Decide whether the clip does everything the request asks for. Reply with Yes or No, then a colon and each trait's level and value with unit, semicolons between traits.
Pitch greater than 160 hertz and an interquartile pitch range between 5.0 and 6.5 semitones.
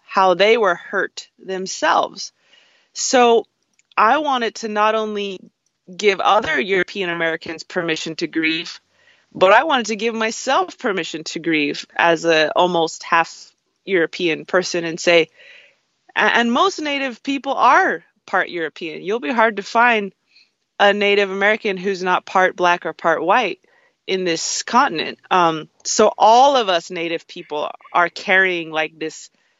Yes: high, 190 Hz; wide, 5.4 semitones